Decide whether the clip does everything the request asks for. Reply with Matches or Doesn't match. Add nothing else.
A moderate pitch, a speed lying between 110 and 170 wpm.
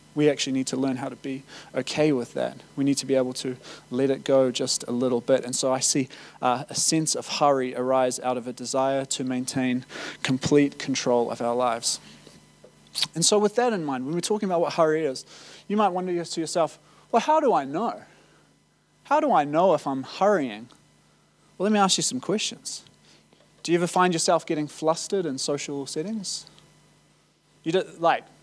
Doesn't match